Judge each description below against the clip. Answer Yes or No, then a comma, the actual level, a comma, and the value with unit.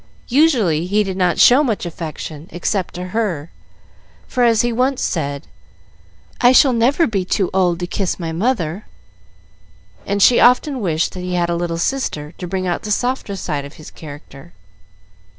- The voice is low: No, medium, 185 Hz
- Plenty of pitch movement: Yes, wide, 5.9 semitones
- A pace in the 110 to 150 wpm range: No, average, 170 wpm